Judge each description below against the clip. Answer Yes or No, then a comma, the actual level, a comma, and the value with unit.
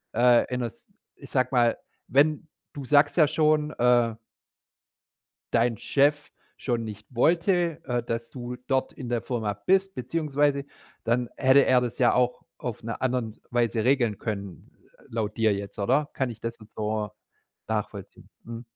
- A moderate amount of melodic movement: Yes, average, 3.5 semitones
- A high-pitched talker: No, low, 125 Hz